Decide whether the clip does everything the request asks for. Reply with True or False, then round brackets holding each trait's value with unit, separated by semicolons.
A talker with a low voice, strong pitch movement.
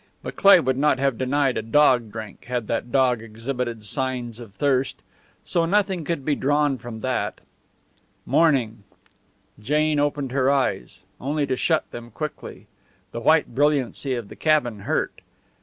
False (130 Hz; 3.7 semitones)